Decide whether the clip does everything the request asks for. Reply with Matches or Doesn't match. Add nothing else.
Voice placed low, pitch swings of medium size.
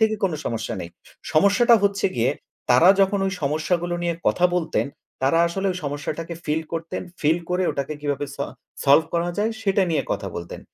Doesn't match